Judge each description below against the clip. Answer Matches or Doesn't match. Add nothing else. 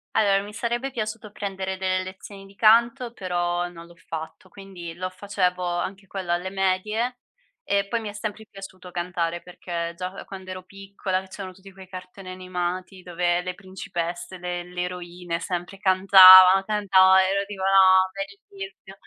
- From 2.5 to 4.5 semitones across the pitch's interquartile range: Doesn't match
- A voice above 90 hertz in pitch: Matches